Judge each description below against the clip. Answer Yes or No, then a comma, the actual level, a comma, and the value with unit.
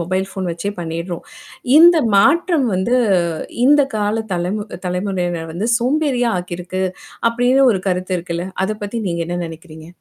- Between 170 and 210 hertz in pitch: Yes, high, 190 Hz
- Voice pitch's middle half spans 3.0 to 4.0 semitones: No, average, 5.3 semitones